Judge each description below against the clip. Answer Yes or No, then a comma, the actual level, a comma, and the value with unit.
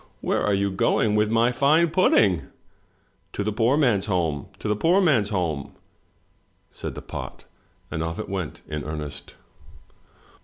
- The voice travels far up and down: Yes, wide, 6.3 semitones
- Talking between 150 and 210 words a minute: Yes, average, 160 wpm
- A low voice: Yes, low, 100 Hz